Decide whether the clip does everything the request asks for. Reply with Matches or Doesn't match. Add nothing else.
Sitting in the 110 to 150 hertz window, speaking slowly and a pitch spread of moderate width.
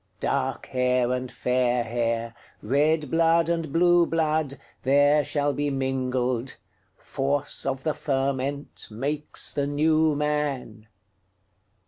Matches